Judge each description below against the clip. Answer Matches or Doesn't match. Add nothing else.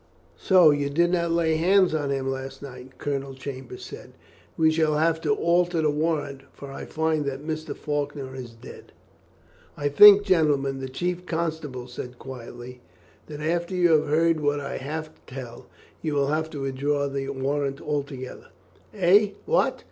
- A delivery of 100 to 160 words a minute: Doesn't match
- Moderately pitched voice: Matches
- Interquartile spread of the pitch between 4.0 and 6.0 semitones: Doesn't match